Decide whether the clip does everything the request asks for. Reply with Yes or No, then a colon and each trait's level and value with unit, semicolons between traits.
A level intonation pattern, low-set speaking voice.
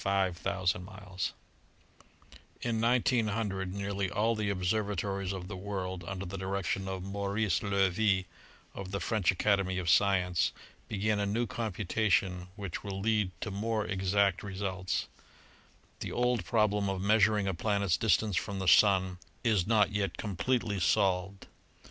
Yes: narrow, 2.1 semitones; low, 100 Hz